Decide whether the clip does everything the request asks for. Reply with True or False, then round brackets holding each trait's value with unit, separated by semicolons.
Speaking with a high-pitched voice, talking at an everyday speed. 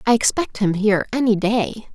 True (215 Hz; 185 wpm)